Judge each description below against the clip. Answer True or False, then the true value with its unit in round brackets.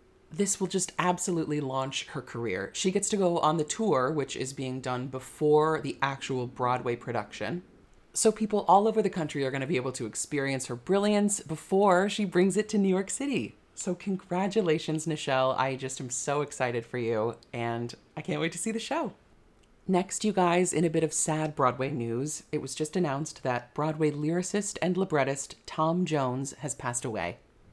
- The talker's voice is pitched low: False (155 Hz)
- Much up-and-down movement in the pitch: True (6.0 semitones)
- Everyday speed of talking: True (190 wpm)